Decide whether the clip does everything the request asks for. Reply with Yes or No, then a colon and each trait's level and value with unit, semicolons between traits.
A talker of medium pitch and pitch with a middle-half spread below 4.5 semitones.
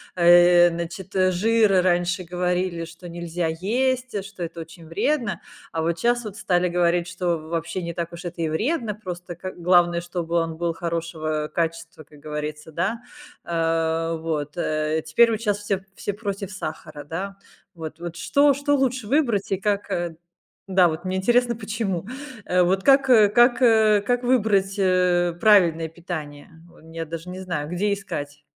Yes: medium, 175 Hz; average, 3.7 semitones